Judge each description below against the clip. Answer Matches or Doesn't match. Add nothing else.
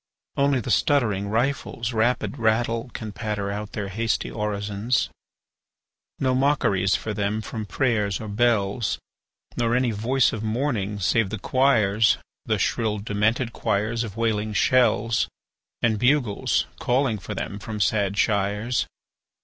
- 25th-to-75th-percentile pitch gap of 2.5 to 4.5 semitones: Matches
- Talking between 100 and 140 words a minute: Matches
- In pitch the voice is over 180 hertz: Doesn't match